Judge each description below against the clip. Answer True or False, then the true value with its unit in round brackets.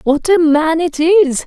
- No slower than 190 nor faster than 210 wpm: True (205 wpm)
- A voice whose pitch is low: False (325 Hz)